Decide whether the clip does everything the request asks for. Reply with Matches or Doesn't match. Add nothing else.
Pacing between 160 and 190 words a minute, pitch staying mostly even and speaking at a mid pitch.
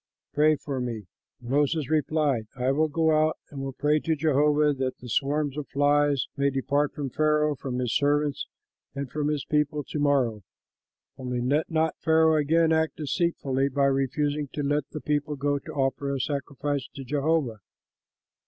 Matches